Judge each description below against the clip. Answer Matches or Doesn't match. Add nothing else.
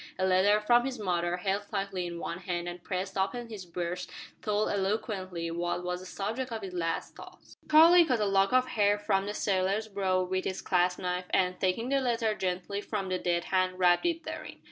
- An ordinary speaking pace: Doesn't match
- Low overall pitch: Doesn't match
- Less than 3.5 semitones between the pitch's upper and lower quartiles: Matches